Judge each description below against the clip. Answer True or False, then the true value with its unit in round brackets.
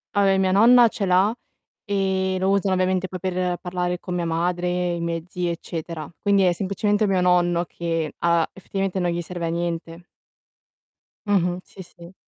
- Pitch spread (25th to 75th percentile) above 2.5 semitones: False (1.9 semitones)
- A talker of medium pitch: True (180 Hz)